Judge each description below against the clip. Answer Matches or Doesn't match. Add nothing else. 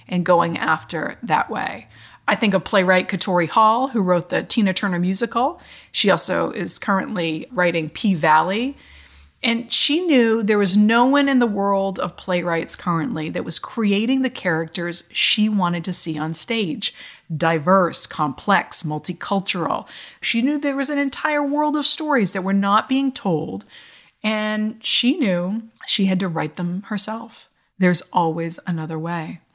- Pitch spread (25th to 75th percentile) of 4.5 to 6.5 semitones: Matches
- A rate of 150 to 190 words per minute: Matches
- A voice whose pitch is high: Matches